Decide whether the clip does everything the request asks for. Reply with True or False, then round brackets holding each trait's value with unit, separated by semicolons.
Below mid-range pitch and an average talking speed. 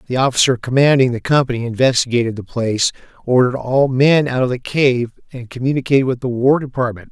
True (125 Hz; 175 wpm)